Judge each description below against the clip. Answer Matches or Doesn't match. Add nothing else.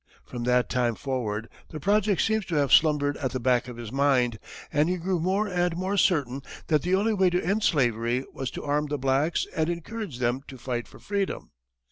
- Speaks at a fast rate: Matches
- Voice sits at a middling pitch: Matches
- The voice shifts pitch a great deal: Matches